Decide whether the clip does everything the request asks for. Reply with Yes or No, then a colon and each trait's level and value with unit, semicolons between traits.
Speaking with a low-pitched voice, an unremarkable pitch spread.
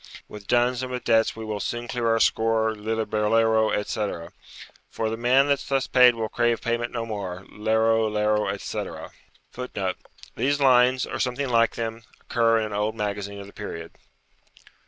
No: low, 115 Hz; narrow, 2.2 semitones